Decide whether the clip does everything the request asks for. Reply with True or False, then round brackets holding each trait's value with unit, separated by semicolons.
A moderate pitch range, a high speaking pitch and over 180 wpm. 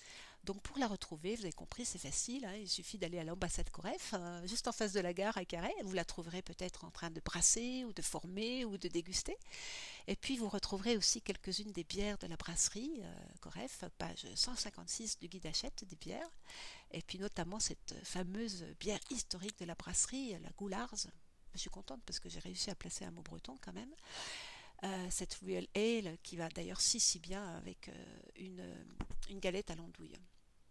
True (4.5 semitones; 195 Hz; 200 wpm)